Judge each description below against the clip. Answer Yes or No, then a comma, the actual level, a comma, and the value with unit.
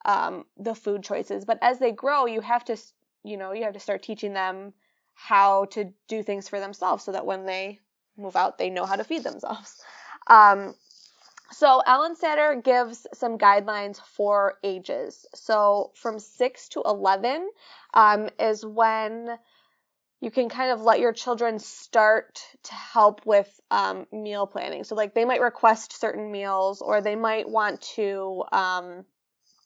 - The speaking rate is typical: Yes, average, 165 wpm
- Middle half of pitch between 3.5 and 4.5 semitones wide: No, average, 2.7 semitones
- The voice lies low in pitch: No, high, 215 Hz